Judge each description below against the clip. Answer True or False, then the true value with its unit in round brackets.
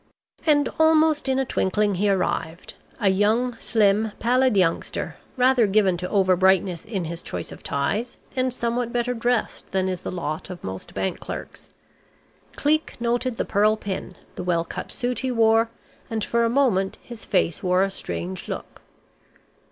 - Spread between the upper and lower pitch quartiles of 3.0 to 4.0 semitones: False (4.6 semitones)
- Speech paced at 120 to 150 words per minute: False (165 wpm)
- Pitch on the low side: False (215 Hz)